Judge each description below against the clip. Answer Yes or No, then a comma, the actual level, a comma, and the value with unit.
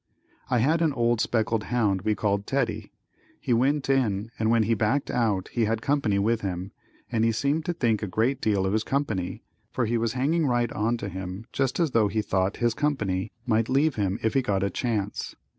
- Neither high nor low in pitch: No, low, 115 Hz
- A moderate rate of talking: No, fast, 215 wpm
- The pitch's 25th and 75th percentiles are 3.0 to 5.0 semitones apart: Yes, average, 3.9 semitones